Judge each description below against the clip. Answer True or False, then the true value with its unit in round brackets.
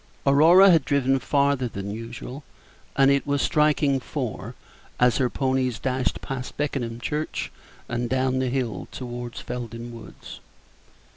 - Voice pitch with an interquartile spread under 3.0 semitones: True (2.6 semitones)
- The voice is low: True (130 Hz)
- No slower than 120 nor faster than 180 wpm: True (135 wpm)